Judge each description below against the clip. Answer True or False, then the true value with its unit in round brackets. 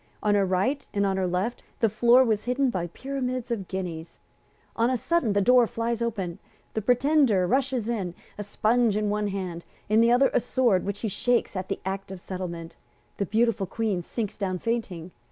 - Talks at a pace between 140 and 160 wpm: False (195 wpm)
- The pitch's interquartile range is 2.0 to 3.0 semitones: False (4.1 semitones)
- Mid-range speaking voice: False (210 Hz)